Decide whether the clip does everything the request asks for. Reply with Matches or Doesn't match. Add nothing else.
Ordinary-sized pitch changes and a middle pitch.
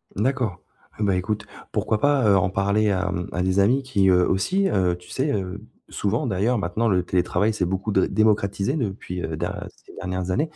Doesn't match